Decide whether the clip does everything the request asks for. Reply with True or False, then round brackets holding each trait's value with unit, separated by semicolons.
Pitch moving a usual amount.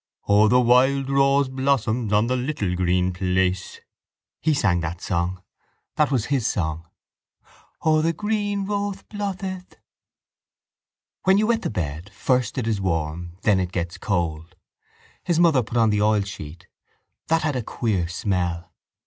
False (7.8 semitones)